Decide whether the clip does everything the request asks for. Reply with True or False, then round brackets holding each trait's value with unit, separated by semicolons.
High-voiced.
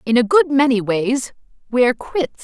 True (250 Hz)